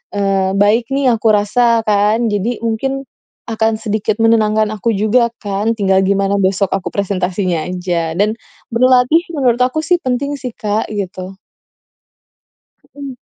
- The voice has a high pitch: Yes, high, 215 Hz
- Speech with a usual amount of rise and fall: Yes, average, 3.5 semitones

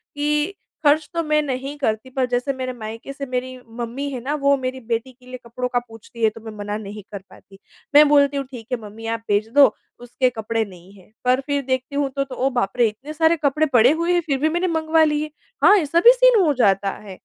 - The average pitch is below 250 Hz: No, very high, 260 Hz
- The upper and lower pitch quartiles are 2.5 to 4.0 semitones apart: No, average, 4.6 semitones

